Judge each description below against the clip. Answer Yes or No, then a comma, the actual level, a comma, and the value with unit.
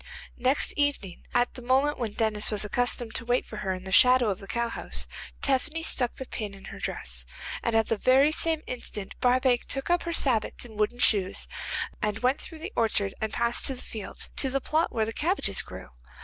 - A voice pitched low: No, high, 245 Hz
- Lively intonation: No, average, 4.0 semitones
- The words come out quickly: Yes, fast, 210 wpm